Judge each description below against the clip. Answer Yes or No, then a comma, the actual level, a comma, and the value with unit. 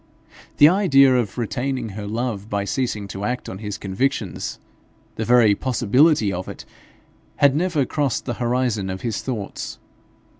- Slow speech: No, average, 150 wpm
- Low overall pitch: Yes, low, 120 Hz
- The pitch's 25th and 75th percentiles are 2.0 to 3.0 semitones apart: No, average, 4.6 semitones